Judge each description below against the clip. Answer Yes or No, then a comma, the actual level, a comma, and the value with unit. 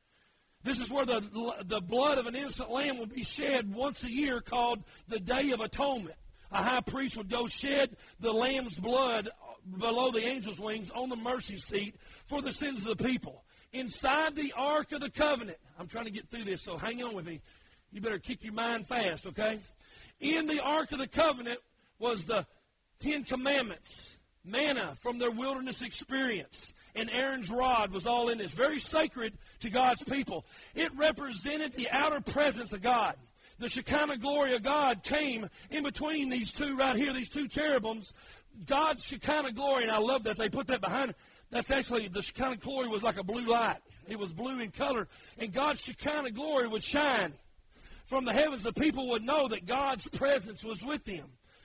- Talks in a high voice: Yes, very high, 250 Hz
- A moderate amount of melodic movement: Yes, average, 3.8 semitones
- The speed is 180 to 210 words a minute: Yes, average, 190 wpm